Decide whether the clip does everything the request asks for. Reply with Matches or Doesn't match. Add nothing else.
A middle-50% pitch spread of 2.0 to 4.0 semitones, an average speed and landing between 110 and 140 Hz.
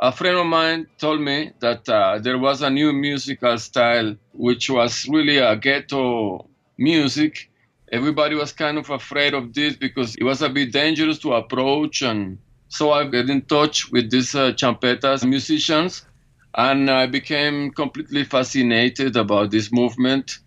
Matches